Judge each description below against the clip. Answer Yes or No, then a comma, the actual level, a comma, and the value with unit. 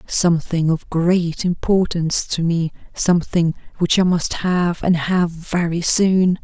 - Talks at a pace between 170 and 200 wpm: No, average, 140 wpm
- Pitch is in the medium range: Yes, medium, 170 Hz